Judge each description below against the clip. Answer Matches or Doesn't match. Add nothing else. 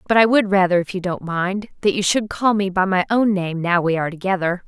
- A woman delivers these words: Matches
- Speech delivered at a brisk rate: Matches